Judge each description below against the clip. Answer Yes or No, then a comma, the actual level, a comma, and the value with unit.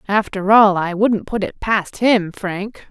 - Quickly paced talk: No, average, 185 wpm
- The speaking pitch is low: No, high, 200 Hz